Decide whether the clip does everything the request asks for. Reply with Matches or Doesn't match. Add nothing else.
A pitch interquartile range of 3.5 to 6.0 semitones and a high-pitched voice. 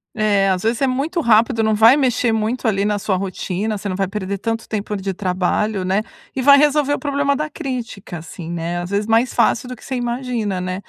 Matches